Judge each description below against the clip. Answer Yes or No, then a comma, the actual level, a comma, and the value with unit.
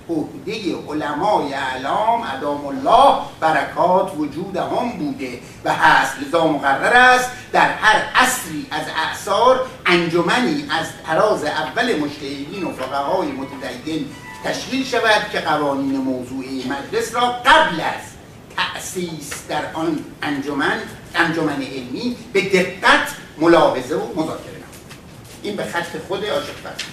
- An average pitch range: No, wide, 7.7 semitones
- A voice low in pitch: No, medium, 160 Hz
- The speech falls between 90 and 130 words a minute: Yes, average, 120 wpm